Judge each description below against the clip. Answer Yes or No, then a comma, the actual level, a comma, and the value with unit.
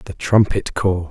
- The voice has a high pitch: No, very low, 95 Hz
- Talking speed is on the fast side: No, average, 165 wpm